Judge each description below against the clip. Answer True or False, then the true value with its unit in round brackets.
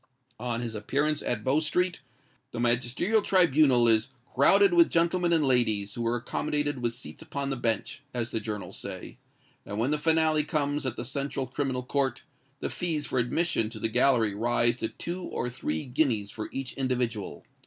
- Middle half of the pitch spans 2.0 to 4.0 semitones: False (4.5 semitones)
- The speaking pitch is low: True (130 Hz)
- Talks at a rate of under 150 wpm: False (180 wpm)